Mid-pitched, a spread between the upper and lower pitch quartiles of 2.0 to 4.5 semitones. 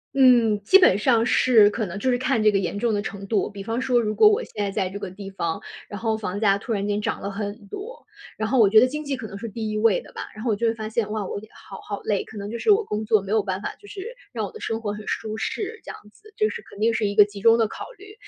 No: high, 220 Hz; average, 3.1 semitones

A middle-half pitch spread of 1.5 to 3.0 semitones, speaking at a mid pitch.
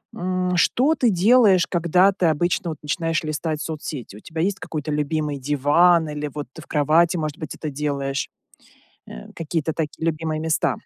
Yes: average, 2.7 semitones; medium, 160 Hz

